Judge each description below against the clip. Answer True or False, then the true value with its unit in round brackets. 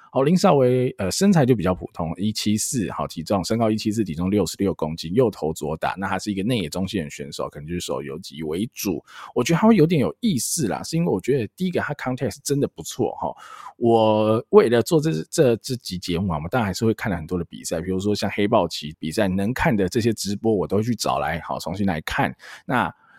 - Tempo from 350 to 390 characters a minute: True (360 characters per minute)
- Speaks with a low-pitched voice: True (105 Hz)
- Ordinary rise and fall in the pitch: False (5.9 semitones)